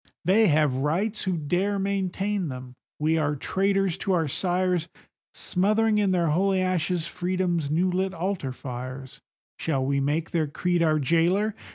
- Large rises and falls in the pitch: No, average, 4.0 semitones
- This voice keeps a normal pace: Yes, average, 155 wpm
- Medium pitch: Yes, medium, 175 Hz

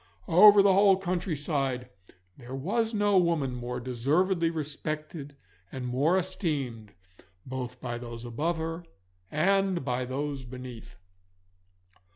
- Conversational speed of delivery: No, slow, 115 wpm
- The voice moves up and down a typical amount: No, wide, 6.2 semitones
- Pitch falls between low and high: Yes, medium, 150 Hz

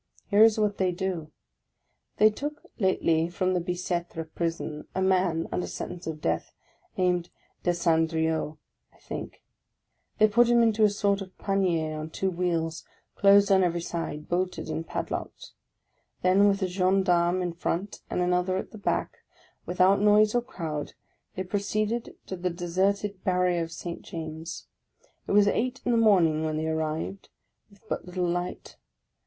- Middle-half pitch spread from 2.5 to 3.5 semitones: Yes, average, 3.1 semitones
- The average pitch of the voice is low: No, medium, 180 Hz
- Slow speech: No, average, 160 wpm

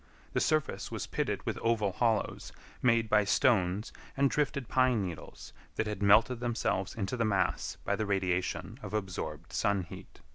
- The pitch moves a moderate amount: Yes, average, 3.6 semitones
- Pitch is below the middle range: Yes, low, 105 Hz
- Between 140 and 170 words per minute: Yes, average, 160 wpm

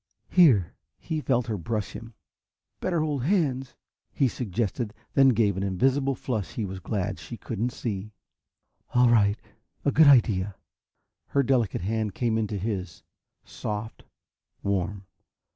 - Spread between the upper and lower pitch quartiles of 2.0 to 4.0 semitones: No, average, 4.5 semitones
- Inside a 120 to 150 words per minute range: Yes, slow, 135 wpm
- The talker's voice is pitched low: Yes, low, 115 Hz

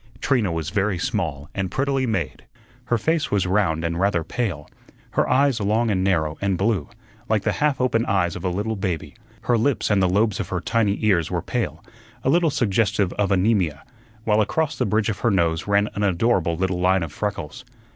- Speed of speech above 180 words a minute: Yes, average, 200 wpm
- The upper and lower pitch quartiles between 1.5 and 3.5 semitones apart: No, average, 4.3 semitones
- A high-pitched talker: No, low, 100 Hz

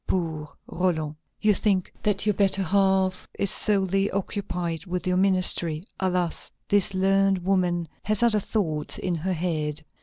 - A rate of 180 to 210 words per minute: No, average, 145 wpm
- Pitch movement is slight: Yes, narrow, 2.3 semitones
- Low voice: No, medium, 185 Hz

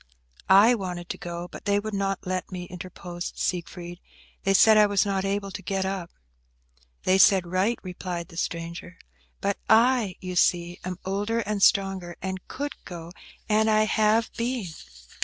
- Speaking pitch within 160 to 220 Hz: Yes, high, 190 Hz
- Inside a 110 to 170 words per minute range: Yes, average, 165 wpm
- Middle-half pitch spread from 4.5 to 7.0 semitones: No, average, 2.7 semitones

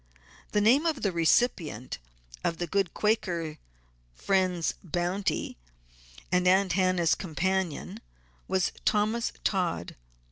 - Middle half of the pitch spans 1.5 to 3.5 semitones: Yes, average, 2.8 semitones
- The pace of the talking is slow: Yes, slow, 105 wpm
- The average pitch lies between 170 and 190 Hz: Yes, medium, 185 Hz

